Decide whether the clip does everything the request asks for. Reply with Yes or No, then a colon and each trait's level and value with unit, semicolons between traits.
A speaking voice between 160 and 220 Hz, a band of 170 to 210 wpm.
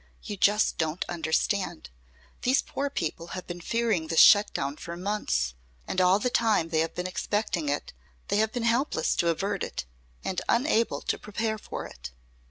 Yes: high, 190 Hz; average, 180 wpm